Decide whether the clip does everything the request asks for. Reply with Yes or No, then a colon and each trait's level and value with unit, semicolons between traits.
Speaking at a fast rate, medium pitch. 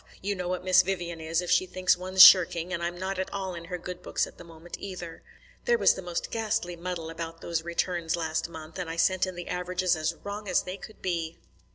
Yes: fast, 240 wpm; medium, 180 Hz